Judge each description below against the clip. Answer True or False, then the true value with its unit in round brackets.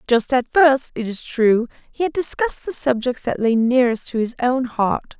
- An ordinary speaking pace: False (210 wpm)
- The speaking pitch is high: True (255 Hz)